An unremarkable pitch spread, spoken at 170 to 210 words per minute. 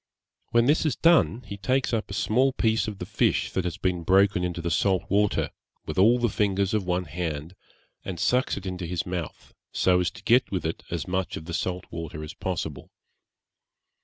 Yes: average, 3.7 semitones; fast, 205 wpm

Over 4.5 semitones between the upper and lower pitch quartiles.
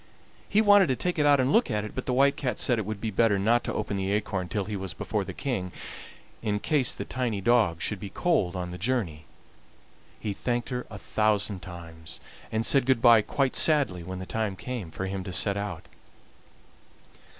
Yes: average, 4.9 semitones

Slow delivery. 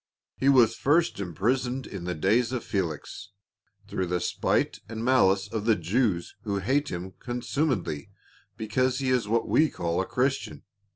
No: average, 160 wpm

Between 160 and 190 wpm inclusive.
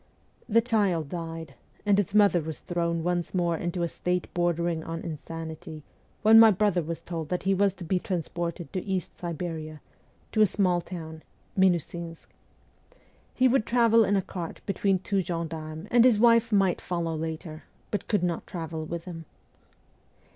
Yes: average, 165 wpm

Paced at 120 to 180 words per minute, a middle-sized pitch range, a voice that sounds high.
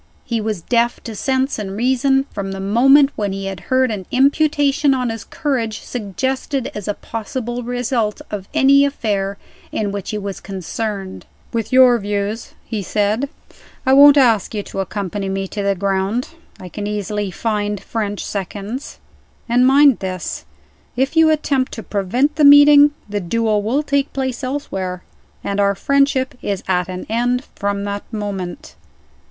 Yes: average, 160 wpm; average, 4.8 semitones; high, 220 Hz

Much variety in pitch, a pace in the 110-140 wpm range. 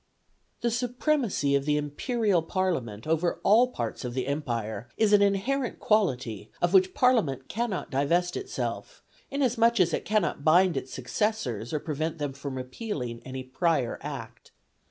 No: wide, 8.7 semitones; average, 150 wpm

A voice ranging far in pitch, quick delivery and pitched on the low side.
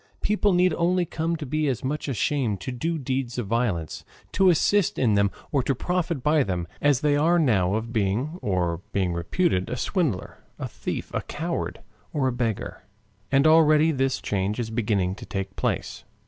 No: wide, 7.3 semitones; average, 185 wpm; low, 130 Hz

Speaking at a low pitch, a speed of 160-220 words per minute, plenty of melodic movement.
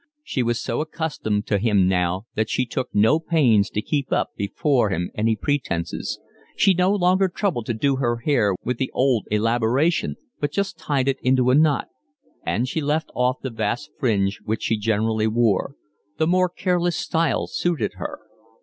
Yes: low, 125 Hz; average, 175 wpm; wide, 6.1 semitones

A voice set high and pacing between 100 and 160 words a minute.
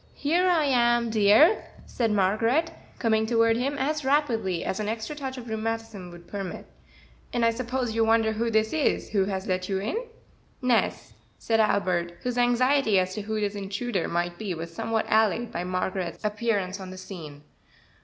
No: high, 220 Hz; average, 175 wpm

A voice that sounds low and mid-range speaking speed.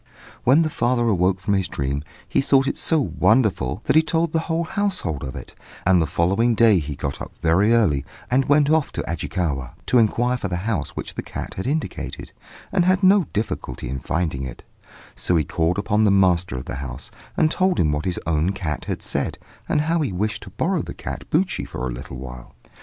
No: low, 100 Hz; fast, 215 wpm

